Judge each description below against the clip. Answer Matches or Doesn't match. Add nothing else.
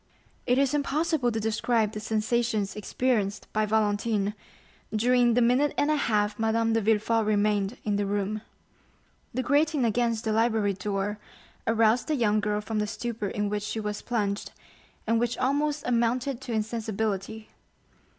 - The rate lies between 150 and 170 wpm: Matches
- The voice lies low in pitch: Doesn't match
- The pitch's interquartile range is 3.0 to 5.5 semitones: Doesn't match